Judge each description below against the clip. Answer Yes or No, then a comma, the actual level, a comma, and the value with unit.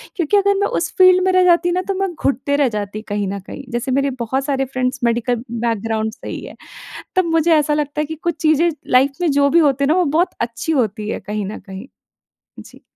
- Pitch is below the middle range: No, very high, 275 Hz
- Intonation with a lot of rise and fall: Yes, wide, 6.6 semitones